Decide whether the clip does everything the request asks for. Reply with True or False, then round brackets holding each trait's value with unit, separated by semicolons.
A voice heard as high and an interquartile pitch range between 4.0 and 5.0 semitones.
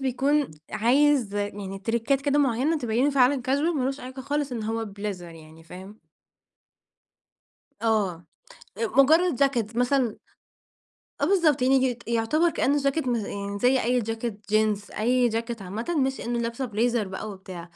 True (235 Hz; 4.4 semitones)